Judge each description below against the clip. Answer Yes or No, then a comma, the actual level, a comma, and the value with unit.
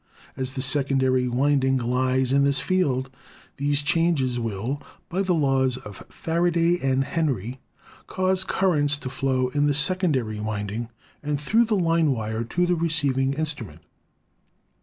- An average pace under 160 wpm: Yes, average, 140 wpm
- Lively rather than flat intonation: No, average, 4.2 semitones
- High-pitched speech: No, medium, 140 Hz